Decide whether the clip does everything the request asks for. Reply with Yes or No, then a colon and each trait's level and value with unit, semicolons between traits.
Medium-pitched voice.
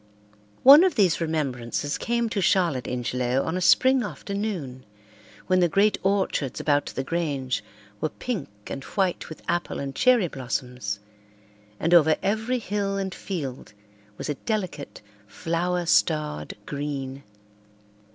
Yes: medium, 165 Hz